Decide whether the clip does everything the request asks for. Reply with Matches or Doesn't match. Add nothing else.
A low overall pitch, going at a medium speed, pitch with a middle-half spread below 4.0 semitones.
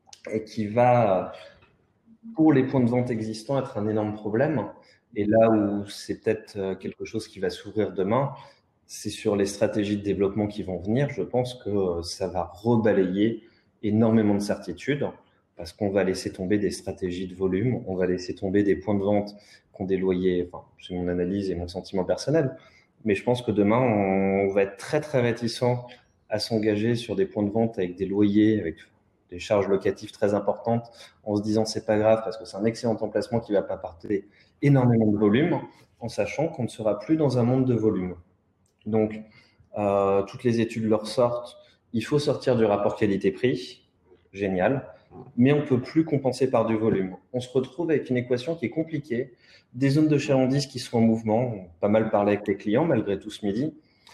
Matches